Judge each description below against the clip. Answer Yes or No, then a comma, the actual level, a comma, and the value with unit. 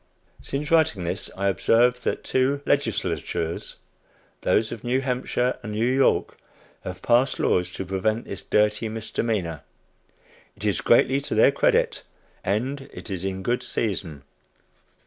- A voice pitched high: No, low, 115 Hz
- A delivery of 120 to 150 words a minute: Yes, average, 140 wpm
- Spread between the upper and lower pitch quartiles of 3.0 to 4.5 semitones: No, average, 5.1 semitones